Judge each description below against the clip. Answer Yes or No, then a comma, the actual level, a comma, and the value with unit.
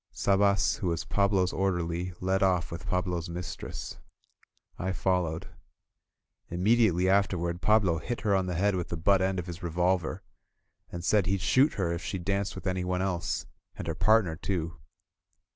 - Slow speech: No, average, 160 wpm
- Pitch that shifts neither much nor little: No, narrow, 2.2 semitones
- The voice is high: No, very low, 90 Hz